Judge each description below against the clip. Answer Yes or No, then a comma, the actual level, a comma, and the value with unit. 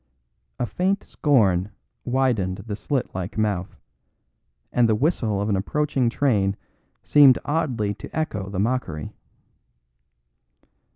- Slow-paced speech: Yes, slow, 115 wpm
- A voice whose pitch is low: Yes, low, 110 Hz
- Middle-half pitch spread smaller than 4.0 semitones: No, wide, 5.6 semitones